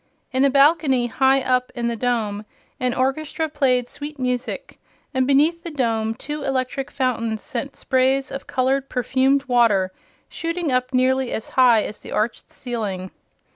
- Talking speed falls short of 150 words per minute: No, average, 155 wpm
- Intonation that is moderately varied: No, narrow, 2.3 semitones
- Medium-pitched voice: No, very high, 260 Hz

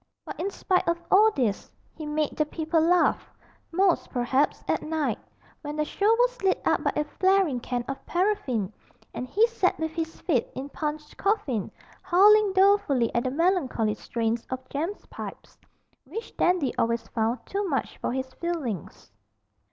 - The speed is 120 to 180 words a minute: Yes, average, 165 wpm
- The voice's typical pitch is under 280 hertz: No, very high, 310 Hz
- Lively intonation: Yes, wide, 6.7 semitones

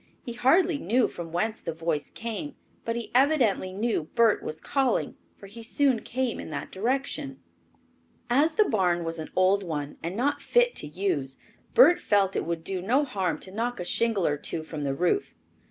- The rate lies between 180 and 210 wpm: Yes, average, 190 wpm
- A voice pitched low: No, high, 210 Hz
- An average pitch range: No, wide, 7.0 semitones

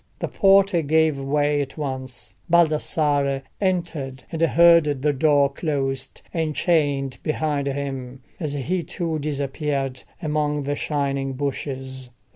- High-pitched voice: No, medium, 145 Hz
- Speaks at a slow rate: Yes, slow, 120 wpm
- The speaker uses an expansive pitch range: No, narrow, 2.6 semitones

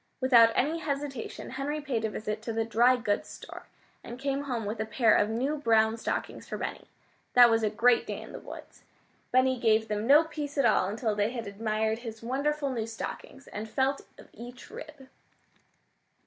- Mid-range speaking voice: No, high, 235 Hz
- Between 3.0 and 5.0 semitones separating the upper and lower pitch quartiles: Yes, average, 3.7 semitones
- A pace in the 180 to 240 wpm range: Yes, average, 190 wpm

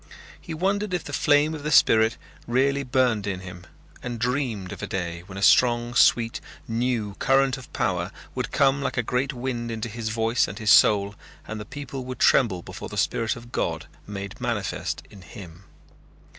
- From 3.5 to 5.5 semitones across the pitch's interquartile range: Yes, average, 4.5 semitones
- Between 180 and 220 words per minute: Yes, average, 185 wpm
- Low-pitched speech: Yes, low, 120 Hz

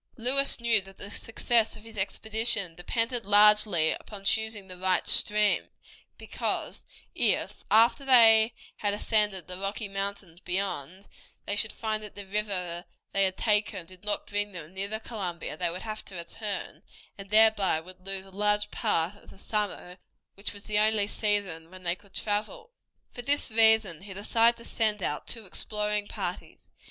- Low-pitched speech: No, high, 205 Hz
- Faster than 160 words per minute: Yes, average, 170 wpm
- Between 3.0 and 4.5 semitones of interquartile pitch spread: No, narrow, 2.6 semitones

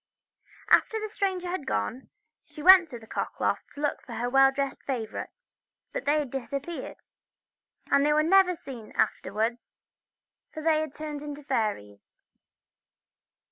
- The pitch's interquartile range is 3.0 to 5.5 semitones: Yes, average, 4.9 semitones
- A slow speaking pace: No, average, 150 wpm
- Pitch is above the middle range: Yes, very high, 285 Hz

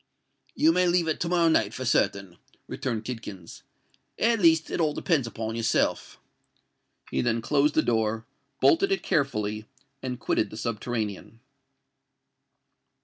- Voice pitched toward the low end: Yes, low, 120 Hz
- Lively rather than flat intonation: Yes, wide, 6.7 semitones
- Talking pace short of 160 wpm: Yes, average, 140 wpm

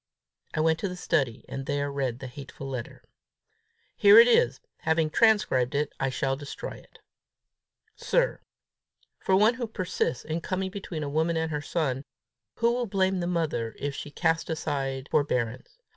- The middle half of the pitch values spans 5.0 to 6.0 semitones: Yes, wide, 5.6 semitones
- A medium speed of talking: Yes, average, 165 wpm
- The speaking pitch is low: No, medium, 155 Hz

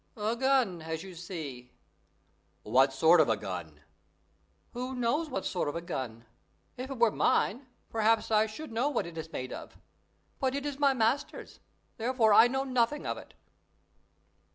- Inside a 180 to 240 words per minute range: No, average, 170 wpm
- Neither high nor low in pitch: No, high, 220 Hz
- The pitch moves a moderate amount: No, wide, 8.1 semitones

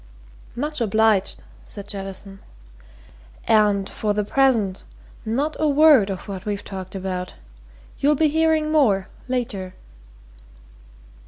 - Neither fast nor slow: No, slow, 110 wpm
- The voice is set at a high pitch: Yes, high, 210 Hz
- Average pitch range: No, wide, 6.3 semitones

